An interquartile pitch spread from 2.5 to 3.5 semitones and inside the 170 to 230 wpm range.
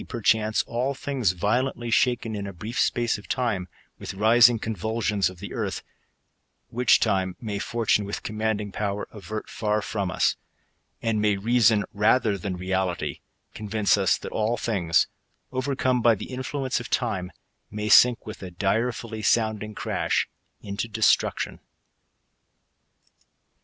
No: average, 2.8 semitones; average, 140 wpm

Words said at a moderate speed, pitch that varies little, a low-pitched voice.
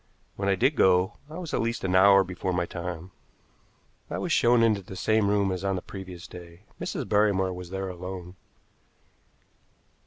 Yes: average, 180 wpm; narrow, 2.2 semitones; very low, 95 Hz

